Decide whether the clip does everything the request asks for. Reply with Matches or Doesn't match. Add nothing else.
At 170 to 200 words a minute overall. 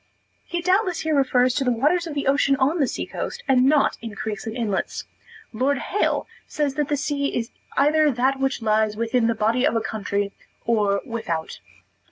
Matches